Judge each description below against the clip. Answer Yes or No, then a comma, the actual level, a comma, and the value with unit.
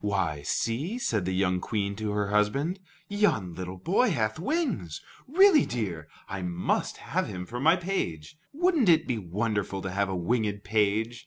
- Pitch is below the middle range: Yes, low, 105 Hz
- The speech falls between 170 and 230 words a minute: Yes, average, 175 wpm